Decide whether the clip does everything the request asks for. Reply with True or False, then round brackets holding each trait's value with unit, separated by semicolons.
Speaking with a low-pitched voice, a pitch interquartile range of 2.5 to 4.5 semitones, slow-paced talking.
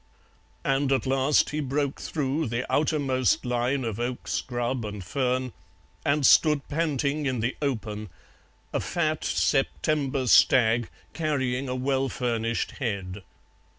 True (130 Hz; 2.9 semitones; 125 wpm)